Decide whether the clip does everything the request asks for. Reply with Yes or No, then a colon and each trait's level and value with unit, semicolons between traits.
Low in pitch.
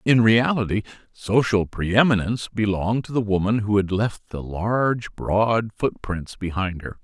Yes: low, 105 Hz